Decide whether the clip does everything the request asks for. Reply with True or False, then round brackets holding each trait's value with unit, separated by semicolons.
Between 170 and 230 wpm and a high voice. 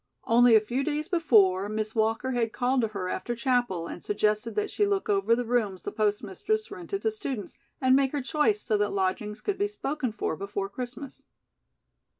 True (190 wpm; 240 Hz)